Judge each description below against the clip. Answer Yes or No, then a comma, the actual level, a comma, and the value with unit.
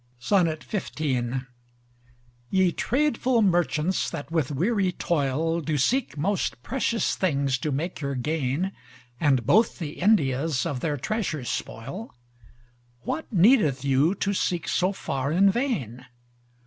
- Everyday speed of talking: No, slow, 120 wpm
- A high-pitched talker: No, medium, 155 Hz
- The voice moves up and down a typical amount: No, wide, 6.6 semitones